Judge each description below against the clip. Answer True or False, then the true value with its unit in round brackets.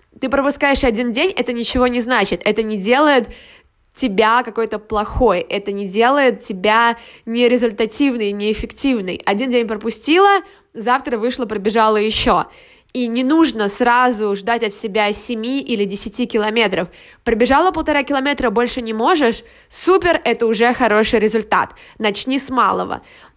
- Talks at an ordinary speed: True (135 wpm)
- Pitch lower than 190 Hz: False (235 Hz)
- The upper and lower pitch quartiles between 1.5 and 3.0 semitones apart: True (2.7 semitones)